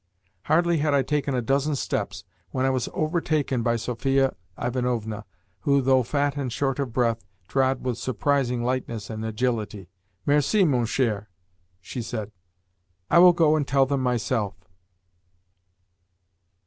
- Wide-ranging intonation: No, average, 3.3 semitones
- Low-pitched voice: Yes, low, 130 Hz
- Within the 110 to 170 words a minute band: Yes, average, 140 wpm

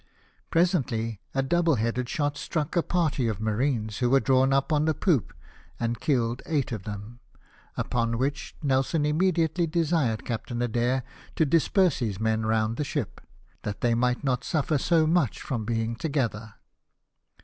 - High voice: No, low, 130 Hz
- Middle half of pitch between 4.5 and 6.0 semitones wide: Yes, average, 5.2 semitones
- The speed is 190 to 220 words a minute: No, average, 160 wpm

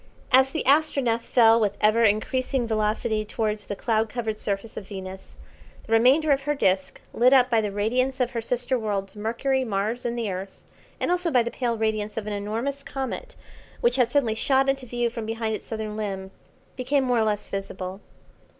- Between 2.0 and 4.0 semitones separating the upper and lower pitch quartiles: Yes, average, 3.3 semitones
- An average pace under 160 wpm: No, average, 195 wpm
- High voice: Yes, high, 230 Hz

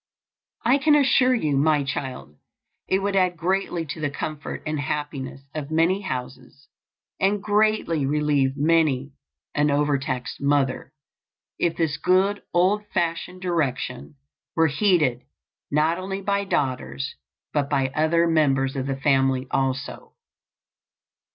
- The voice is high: No, medium, 150 Hz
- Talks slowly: Yes, slow, 125 wpm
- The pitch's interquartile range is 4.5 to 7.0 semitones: Yes, average, 5.2 semitones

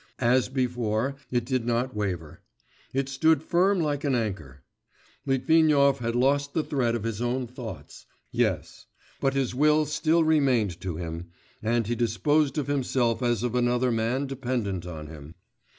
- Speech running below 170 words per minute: Yes, average, 155 wpm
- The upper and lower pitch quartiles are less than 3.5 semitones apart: No, average, 3.9 semitones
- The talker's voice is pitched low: Yes, low, 125 Hz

